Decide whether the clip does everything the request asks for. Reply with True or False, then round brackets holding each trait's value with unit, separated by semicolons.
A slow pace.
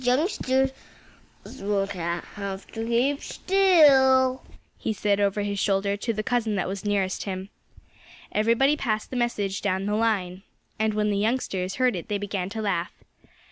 False (160 wpm)